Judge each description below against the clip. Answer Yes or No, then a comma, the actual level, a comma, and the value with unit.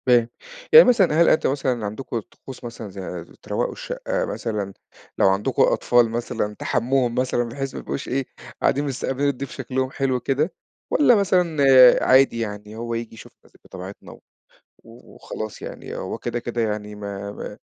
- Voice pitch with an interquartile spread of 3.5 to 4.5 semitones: Yes, average, 4.0 semitones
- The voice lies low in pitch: Yes, low, 120 Hz